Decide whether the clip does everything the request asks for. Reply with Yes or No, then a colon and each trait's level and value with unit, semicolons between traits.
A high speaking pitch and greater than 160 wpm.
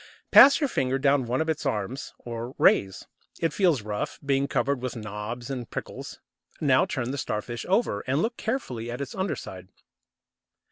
No: low, 130 Hz; average, 170 wpm